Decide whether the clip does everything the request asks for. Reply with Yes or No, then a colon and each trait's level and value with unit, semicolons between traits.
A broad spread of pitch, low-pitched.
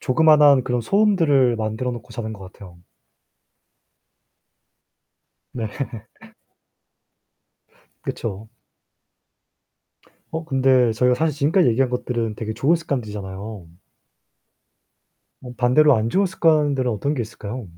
No: average, 5.0 semitones; low, 125 Hz